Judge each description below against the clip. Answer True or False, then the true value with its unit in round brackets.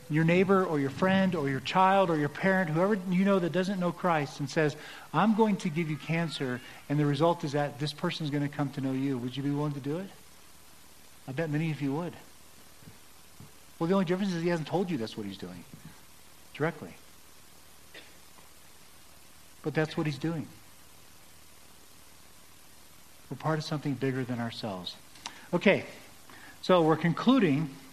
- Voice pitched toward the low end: False (145 Hz)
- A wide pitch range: True (7.4 semitones)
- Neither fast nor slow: True (180 wpm)